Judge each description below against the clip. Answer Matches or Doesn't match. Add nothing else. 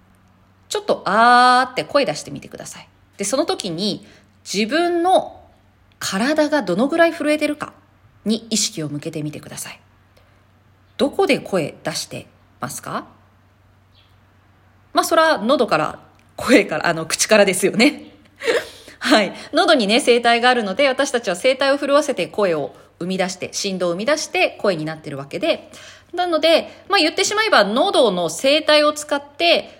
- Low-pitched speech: Doesn't match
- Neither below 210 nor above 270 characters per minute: Doesn't match